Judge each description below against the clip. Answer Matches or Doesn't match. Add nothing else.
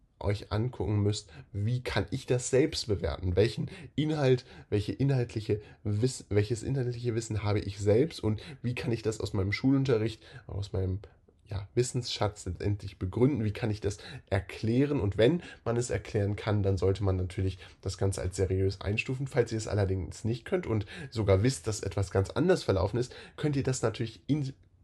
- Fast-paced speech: Doesn't match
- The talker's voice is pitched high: Doesn't match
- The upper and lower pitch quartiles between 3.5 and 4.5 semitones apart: Matches